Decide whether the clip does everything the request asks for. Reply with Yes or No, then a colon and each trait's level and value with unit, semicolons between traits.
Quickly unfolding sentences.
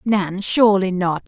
No: average, 140 wpm